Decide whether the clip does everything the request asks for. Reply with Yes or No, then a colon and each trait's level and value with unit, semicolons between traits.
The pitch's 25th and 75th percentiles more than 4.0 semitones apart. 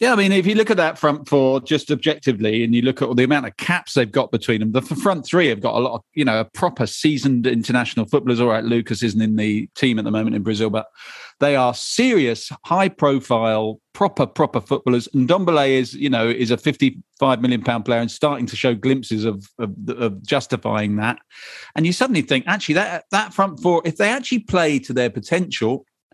Yes: average, 4.7 semitones